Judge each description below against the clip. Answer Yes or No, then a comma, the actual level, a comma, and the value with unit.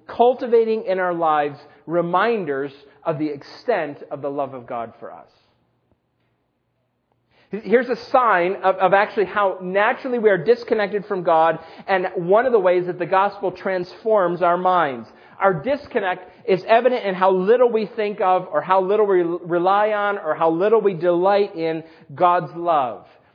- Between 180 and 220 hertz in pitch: Yes, medium, 185 Hz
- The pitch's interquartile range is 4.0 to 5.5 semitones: No, average, 3.4 semitones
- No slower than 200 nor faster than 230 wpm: No, average, 160 wpm